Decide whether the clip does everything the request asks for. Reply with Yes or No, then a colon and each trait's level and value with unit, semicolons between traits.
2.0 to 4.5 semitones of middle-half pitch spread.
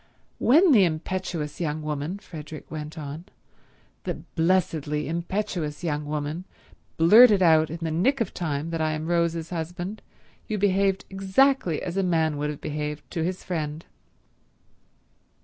Yes: average, 3.6 semitones